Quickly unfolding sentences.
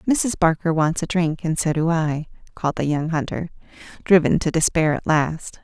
No: average, 190 wpm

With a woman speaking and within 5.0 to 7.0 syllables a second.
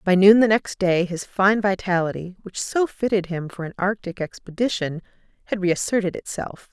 Yes: female; 5.2 syllables/s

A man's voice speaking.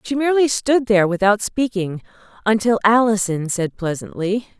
No: female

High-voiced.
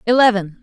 Yes: high, 215 Hz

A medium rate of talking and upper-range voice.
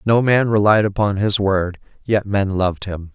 No: average, 190 wpm; low, 100 Hz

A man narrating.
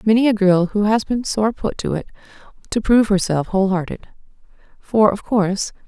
No: female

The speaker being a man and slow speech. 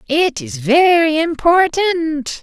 Yes: male; slow, 100 wpm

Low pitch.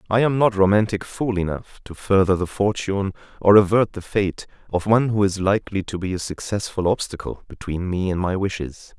Yes: low, 100 Hz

